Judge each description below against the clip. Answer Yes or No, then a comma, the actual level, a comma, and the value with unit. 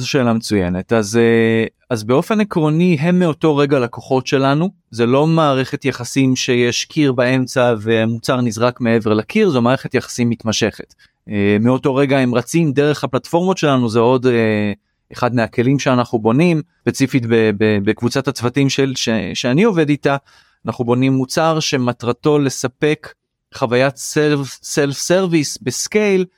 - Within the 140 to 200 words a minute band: No, average, 130 wpm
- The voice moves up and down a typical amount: Yes, average, 3.9 semitones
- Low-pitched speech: Yes, low, 130 Hz